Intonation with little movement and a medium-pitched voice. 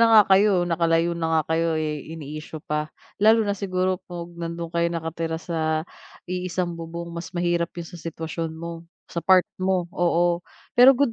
Yes: narrow, 1.7 semitones; medium, 170 Hz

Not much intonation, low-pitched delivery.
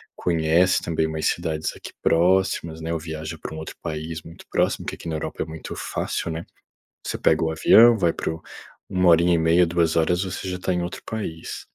Yes: narrow, 1.9 semitones; very low, 80 Hz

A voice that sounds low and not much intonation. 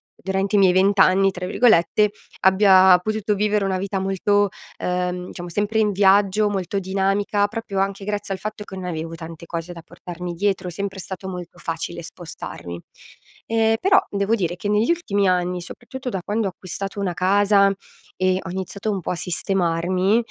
No: high, 195 Hz; narrow, 2.2 semitones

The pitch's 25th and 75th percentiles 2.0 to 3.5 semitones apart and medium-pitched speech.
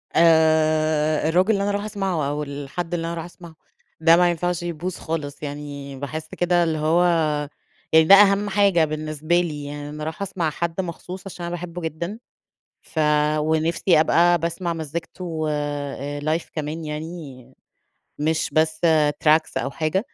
Yes: narrow, 2.4 semitones; medium, 160 Hz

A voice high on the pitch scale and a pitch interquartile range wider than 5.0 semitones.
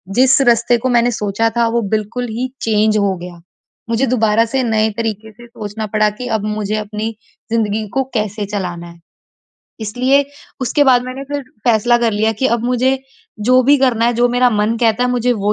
No: high, 230 Hz; average, 2.7 semitones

